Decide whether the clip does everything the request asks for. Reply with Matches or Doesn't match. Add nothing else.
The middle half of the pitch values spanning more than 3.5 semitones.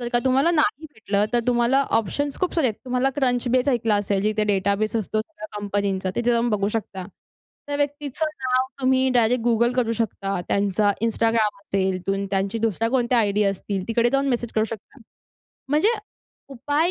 Matches